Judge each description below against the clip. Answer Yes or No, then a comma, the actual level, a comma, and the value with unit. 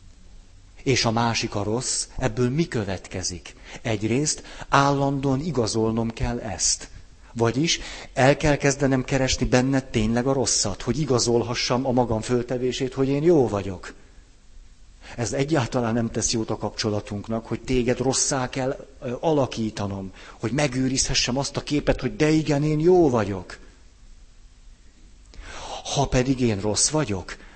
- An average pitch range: Yes, average, 3.5 semitones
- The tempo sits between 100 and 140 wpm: Yes, average, 130 wpm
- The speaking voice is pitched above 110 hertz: Yes, low, 125 Hz